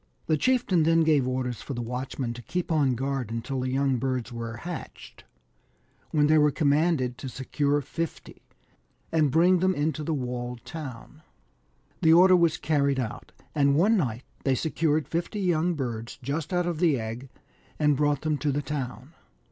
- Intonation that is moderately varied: Yes, average, 4.0 semitones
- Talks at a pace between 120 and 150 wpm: No, average, 170 wpm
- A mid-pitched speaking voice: Yes, medium, 145 Hz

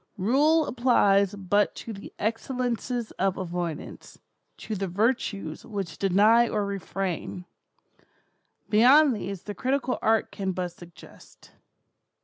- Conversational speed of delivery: No, slow, 110 wpm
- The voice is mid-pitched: No, high, 205 Hz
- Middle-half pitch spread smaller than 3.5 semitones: No, average, 4.0 semitones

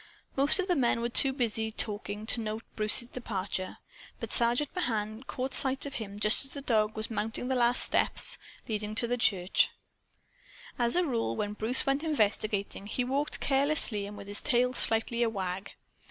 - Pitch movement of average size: Yes, average, 3.8 semitones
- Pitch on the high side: Yes, high, 230 Hz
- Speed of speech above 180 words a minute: Yes, average, 190 wpm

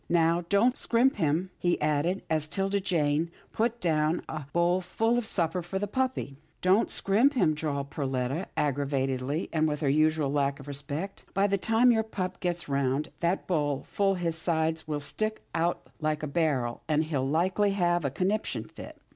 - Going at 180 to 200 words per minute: Yes, average, 190 wpm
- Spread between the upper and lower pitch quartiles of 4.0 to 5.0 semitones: Yes, average, 4.7 semitones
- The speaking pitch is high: No, medium, 165 Hz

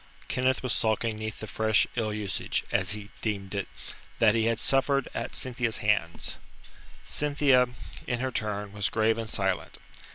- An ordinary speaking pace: Yes, average, 160 wpm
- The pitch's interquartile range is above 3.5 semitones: No, average, 3.0 semitones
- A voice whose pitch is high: No, low, 110 Hz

